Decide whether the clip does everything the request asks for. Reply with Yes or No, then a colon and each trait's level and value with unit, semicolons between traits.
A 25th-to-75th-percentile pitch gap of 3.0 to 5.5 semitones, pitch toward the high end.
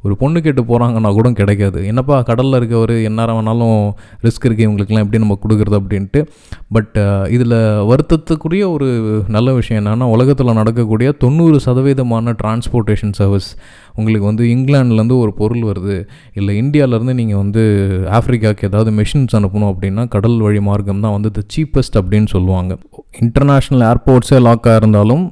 No: average, 3.3 semitones; low, 115 Hz